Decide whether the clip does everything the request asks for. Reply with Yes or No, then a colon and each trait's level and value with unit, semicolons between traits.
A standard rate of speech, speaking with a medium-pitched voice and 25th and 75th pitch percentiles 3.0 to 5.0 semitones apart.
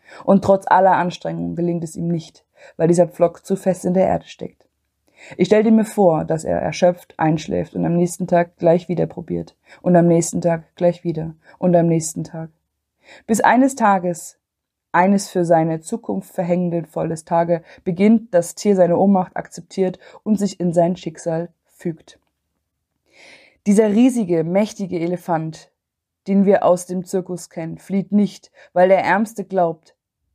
No: average, 160 wpm; medium, 175 Hz; narrow, 2.5 semitones